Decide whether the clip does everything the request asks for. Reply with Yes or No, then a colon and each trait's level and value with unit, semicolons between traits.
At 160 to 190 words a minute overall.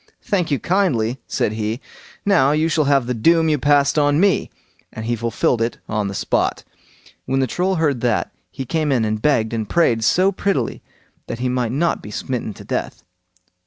No: average, 200 wpm